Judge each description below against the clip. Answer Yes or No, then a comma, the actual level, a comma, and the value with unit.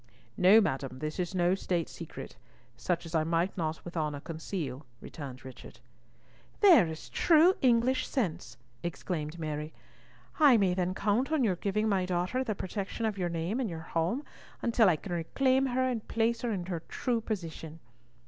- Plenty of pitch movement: Yes, wide, 5.9 semitones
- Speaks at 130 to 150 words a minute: No, average, 175 wpm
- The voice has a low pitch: No, medium, 180 Hz